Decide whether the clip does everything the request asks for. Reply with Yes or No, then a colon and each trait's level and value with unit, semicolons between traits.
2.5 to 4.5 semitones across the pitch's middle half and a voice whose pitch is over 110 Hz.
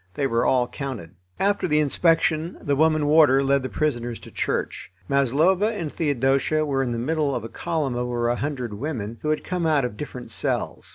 Yes: average, 4.1 semitones; medium, 140 Hz